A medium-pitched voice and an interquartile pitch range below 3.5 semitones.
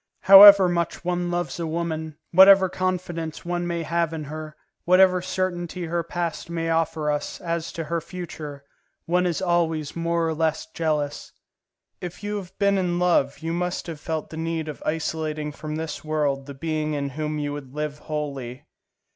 Yes: medium, 165 Hz; narrow, 2.4 semitones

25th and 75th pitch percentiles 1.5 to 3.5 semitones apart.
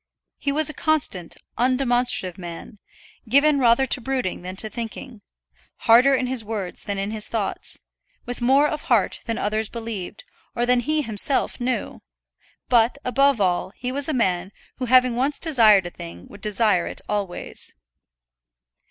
No: average, 4.3 semitones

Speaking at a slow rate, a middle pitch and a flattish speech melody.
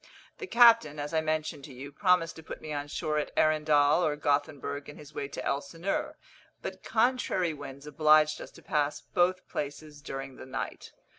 No: average, 180 wpm; medium, 150 Hz; narrow, 2.0 semitones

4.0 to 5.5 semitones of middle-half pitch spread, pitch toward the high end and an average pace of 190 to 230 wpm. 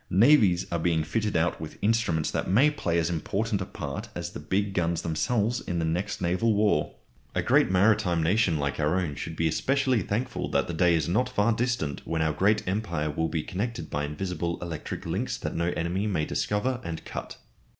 No: average, 4.7 semitones; very low, 90 Hz; average, 200 wpm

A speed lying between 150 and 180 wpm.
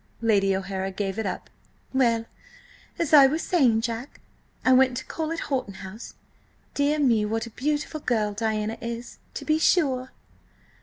Yes: average, 160 wpm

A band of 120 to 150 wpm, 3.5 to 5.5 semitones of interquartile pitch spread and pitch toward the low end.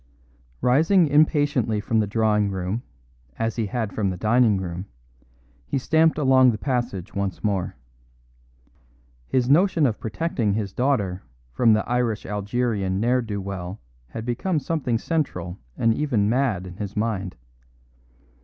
Yes: average, 140 wpm; average, 4.5 semitones; low, 110 Hz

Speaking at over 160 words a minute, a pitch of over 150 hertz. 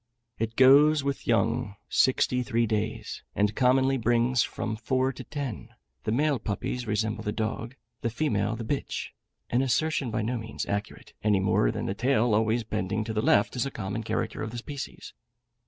No: average, 180 wpm; low, 115 Hz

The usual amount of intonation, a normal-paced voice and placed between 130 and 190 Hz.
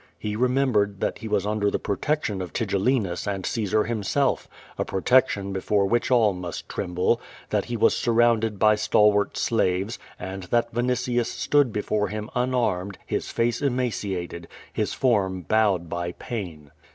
No: average, 3.8 semitones; average, 150 wpm; low, 105 Hz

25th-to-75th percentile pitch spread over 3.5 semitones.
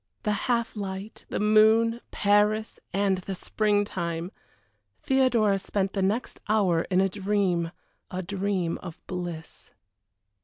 No: narrow, 2.5 semitones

